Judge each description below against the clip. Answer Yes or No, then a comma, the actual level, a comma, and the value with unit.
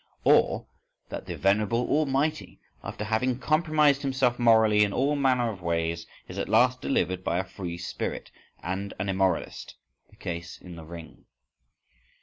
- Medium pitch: No, low, 105 Hz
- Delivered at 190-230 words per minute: No, average, 150 wpm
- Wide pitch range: Yes, wide, 6.5 semitones